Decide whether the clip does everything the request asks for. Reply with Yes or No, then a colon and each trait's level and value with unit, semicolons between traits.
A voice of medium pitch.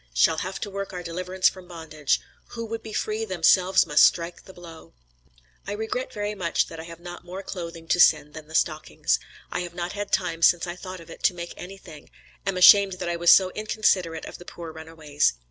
Yes: medium, 175 Hz